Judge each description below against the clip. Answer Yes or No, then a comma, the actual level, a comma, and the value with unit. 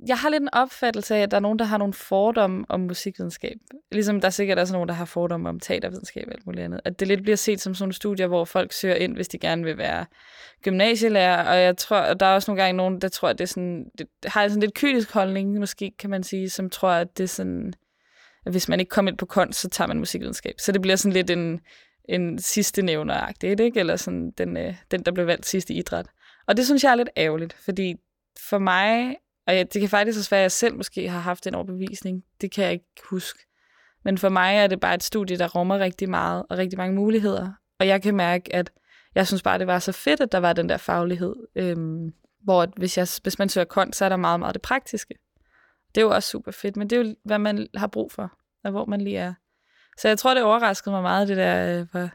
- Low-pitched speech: No, high, 190 Hz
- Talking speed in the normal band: No, fast, 255 wpm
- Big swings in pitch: No, narrow, 2.4 semitones